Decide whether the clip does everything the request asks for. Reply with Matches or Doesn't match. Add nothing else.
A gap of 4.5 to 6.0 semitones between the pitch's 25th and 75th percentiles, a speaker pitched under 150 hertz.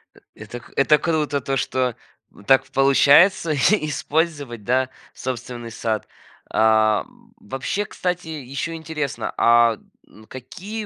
Matches